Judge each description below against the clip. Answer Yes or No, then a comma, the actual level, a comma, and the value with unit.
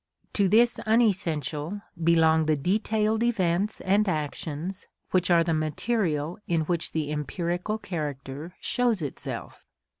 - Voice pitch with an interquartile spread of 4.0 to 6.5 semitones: Yes, average, 4.9 semitones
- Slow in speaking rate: Yes, slow, 120 wpm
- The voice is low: No, medium, 175 Hz